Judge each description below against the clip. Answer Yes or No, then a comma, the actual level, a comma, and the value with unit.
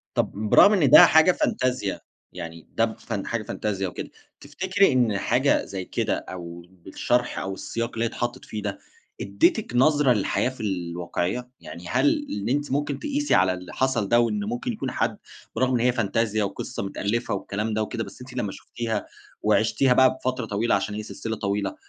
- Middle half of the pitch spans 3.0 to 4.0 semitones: No, average, 4.4 semitones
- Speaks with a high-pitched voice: No, low, 115 Hz